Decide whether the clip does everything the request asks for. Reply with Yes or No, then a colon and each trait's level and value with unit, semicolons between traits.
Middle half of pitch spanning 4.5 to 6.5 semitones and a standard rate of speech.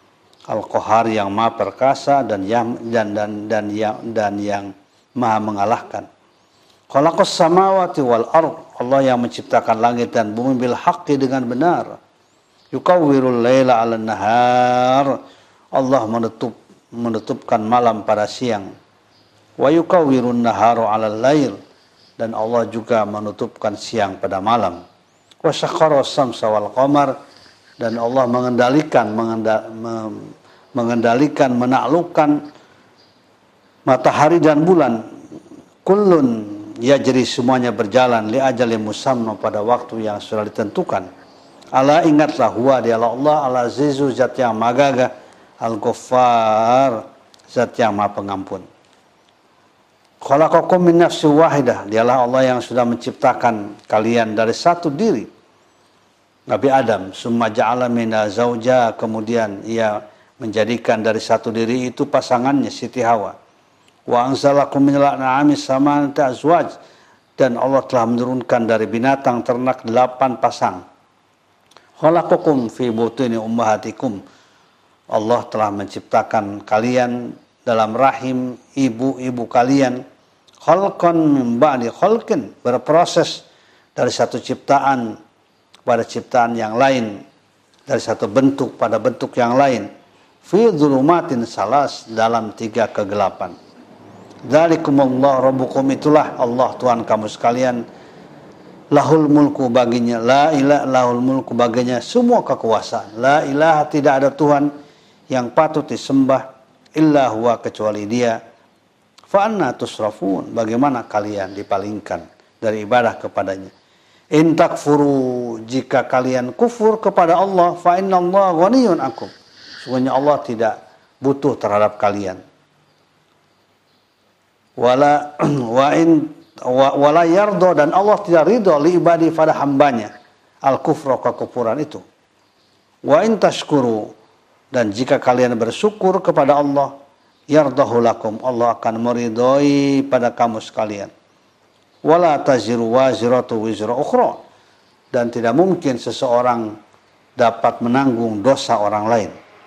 No: average, 3.8 semitones; average, 105 wpm